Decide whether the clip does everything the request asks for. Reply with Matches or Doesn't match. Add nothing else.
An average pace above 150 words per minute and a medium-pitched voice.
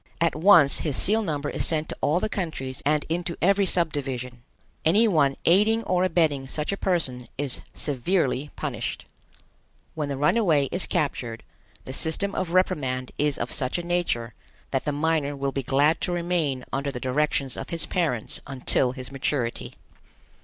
Matches